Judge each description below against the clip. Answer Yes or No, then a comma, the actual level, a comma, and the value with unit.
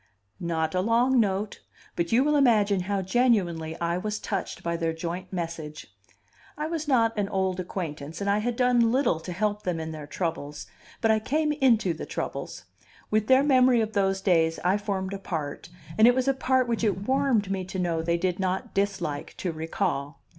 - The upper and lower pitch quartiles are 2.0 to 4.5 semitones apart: No, average, 5.3 semitones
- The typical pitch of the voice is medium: No, high, 195 Hz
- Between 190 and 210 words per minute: Yes, average, 195 wpm